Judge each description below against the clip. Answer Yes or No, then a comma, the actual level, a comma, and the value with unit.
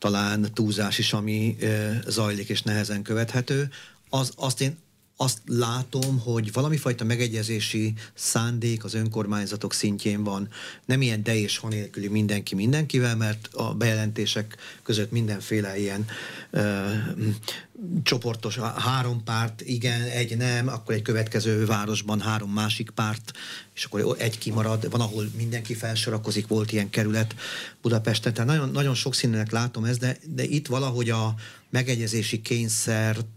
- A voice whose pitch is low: Yes, low, 115 Hz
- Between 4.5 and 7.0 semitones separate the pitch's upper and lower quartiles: No, narrow, 2.4 semitones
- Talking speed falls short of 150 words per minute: Yes, average, 140 wpm